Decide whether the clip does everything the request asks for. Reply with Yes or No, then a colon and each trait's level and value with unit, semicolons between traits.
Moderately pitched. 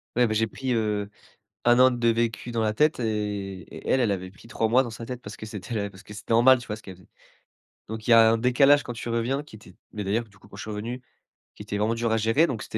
No: low, 115 Hz